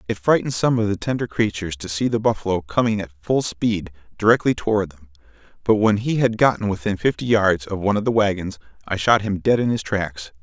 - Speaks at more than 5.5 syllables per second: Yes, 5.9 syllables/s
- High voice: No, low, 100 Hz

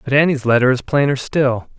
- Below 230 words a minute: Yes, average, 200 wpm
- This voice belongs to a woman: No, male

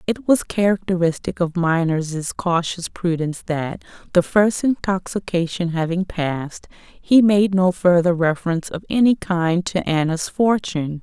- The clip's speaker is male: No, female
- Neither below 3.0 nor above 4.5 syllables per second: Yes, 4.4 syllables/s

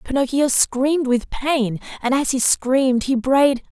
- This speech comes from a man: No, female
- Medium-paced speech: Yes, average, 160 wpm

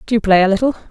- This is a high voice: Yes, high, 210 Hz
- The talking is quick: Yes, fast, 330 wpm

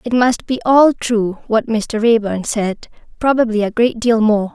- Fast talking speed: No, average, 170 wpm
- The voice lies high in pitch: Yes, high, 225 Hz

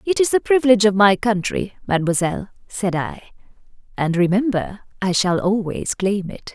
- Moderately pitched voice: No, high, 205 Hz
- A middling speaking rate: Yes, average, 155 wpm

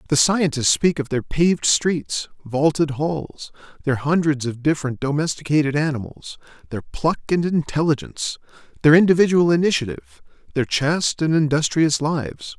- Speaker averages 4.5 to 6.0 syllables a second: Yes, 5.2 syllables/s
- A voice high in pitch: No, medium, 150 Hz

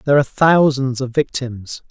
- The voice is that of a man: Yes, male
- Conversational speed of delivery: Yes, average, 160 wpm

